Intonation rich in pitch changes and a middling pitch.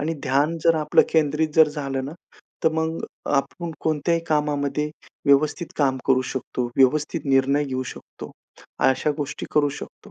No: narrow, 2.4 semitones; medium, 150 Hz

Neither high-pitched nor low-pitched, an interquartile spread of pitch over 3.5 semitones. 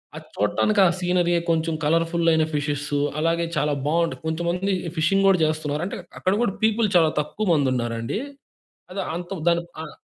No: medium, 165 Hz; average, 2.9 semitones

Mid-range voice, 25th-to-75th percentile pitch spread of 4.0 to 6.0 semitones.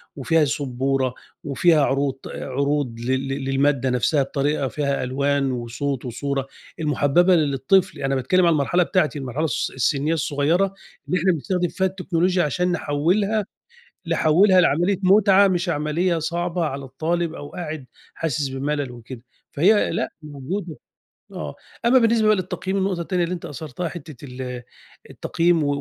Yes: medium, 150 Hz; average, 4.6 semitones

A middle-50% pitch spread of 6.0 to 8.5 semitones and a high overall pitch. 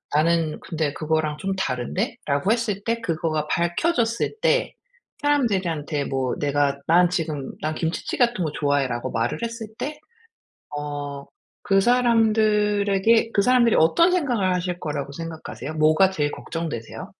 No: wide, 6.9 semitones; medium, 170 Hz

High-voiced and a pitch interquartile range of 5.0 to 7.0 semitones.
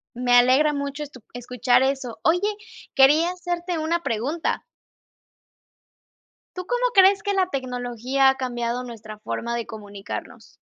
Yes: very high, 265 Hz; wide, 5.6 semitones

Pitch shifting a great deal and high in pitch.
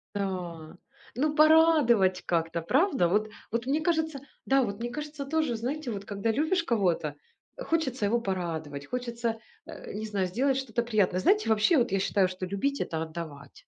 Yes: wide, 7.1 semitones; high, 225 Hz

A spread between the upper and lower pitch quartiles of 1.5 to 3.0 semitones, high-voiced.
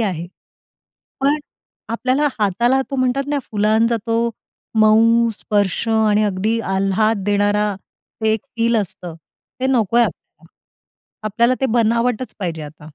Yes: narrow, 2.5 semitones; high, 220 Hz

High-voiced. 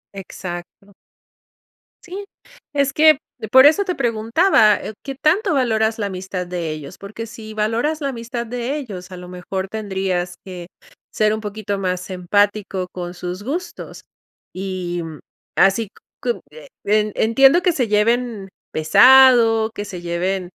Yes: high, 210 Hz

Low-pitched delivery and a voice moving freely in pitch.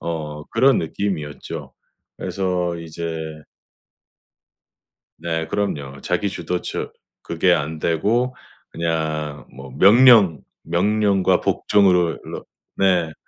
No: very low, 85 Hz; average, 4.2 semitones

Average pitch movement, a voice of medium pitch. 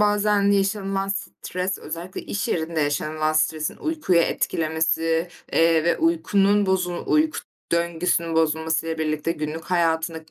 Yes: average, 3.3 semitones; medium, 165 Hz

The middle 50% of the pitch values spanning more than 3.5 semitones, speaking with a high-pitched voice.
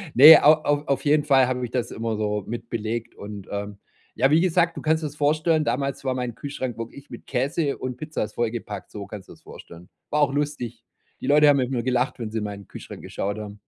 No: average, 4.9 semitones; low, 125 Hz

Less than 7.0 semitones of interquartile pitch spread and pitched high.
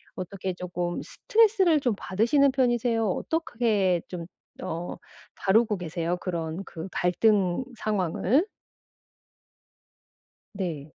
Yes: average, 5.3 semitones; high, 195 Hz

